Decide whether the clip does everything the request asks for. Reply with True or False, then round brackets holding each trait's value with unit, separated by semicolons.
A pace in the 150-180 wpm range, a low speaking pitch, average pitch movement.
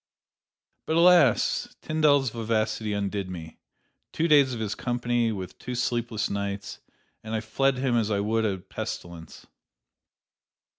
False (135 wpm; 110 Hz; 3.7 semitones)